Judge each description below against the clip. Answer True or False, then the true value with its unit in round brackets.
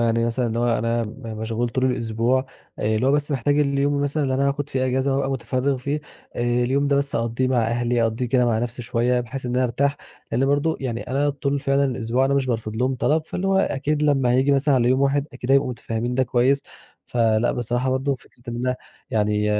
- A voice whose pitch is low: True (130 Hz)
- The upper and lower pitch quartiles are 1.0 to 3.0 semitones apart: True (2.7 semitones)